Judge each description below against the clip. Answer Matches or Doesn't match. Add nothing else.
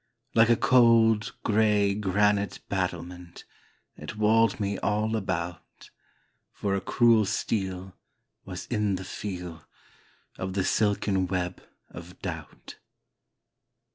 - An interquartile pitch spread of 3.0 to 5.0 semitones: Doesn't match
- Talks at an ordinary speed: Doesn't match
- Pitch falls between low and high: Doesn't match